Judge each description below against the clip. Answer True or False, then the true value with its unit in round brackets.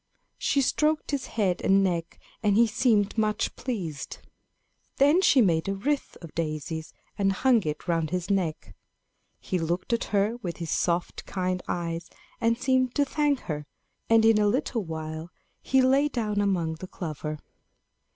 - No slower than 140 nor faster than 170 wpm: True (160 wpm)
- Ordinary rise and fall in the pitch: False (6.3 semitones)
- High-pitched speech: True (195 Hz)